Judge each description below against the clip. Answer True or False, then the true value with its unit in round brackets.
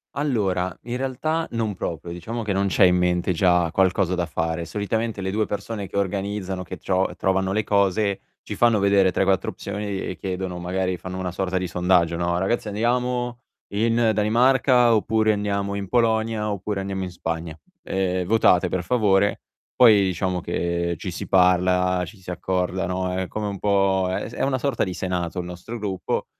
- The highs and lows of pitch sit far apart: False (2.8 semitones)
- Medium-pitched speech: False (95 Hz)